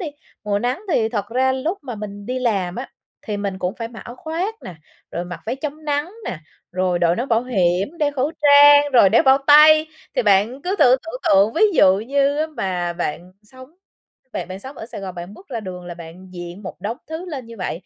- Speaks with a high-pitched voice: Yes, high, 230 Hz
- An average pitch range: No, wide, 7.2 semitones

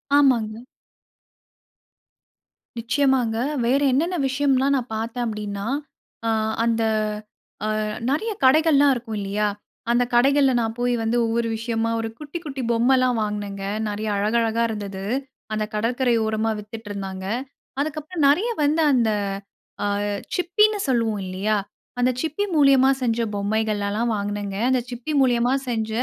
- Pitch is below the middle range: No, high, 235 Hz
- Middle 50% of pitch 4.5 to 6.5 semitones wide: No, average, 4.0 semitones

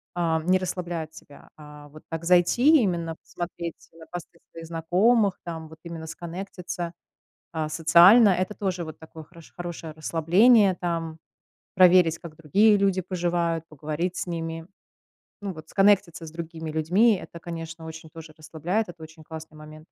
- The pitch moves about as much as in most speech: No, narrow, 2.2 semitones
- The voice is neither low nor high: Yes, medium, 170 Hz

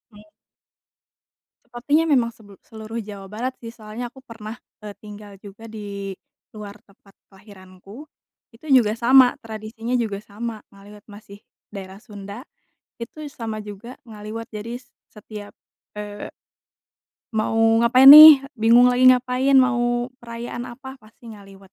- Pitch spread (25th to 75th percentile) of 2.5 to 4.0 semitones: Yes, average, 2.8 semitones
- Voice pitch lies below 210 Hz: No, high, 225 Hz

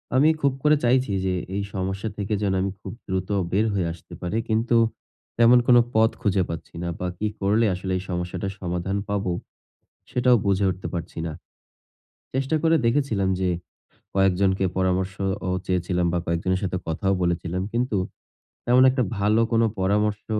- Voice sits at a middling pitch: No, very low, 95 Hz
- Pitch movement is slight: No, average, 3.6 semitones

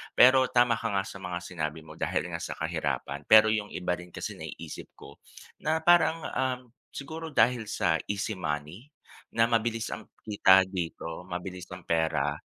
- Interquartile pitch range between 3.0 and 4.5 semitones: No, average, 5.2 semitones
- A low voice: Yes, very low, 95 Hz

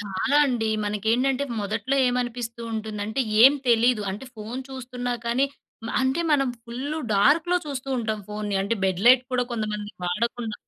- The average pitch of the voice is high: Yes, high, 235 Hz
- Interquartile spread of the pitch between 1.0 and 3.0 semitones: No, average, 3.6 semitones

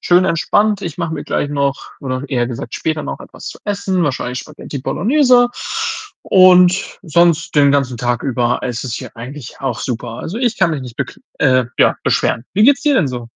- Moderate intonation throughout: No, wide, 6.5 semitones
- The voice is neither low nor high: Yes, medium, 145 Hz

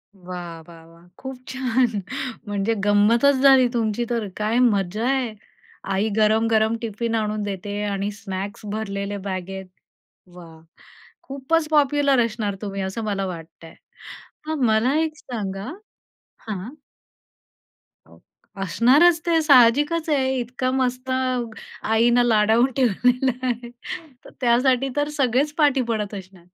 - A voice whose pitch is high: Yes, high, 230 Hz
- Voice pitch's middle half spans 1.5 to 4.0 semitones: No, average, 4.4 semitones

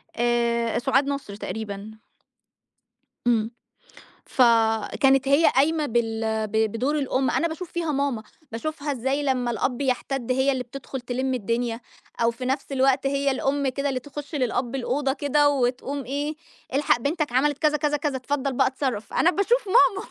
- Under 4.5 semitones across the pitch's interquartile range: Yes, average, 3.2 semitones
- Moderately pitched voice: No, very high, 265 Hz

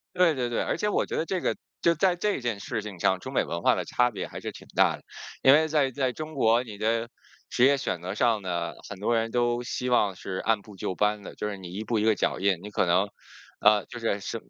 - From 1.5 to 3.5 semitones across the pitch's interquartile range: No, average, 4.2 semitones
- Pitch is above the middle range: No, low, 115 Hz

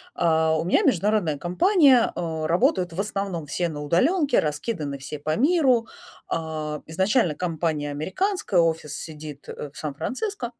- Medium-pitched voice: Yes, medium, 170 Hz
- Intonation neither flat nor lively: No, wide, 6.2 semitones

